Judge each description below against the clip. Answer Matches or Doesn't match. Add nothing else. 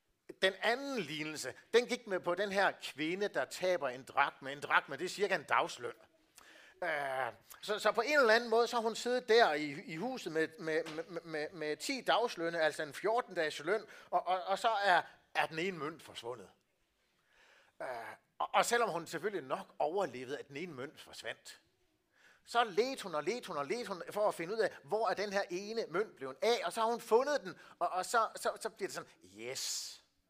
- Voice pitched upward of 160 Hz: Matches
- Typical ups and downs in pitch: Doesn't match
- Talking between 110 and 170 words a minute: Doesn't match